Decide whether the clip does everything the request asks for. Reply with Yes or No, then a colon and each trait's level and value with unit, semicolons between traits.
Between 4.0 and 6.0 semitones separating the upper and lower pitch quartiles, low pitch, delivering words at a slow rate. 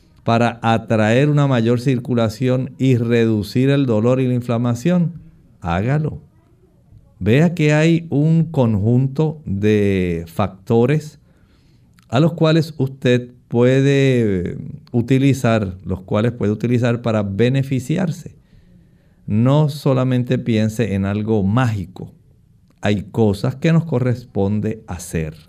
Yes: average, 4.4 semitones; low, 125 Hz; slow, 105 wpm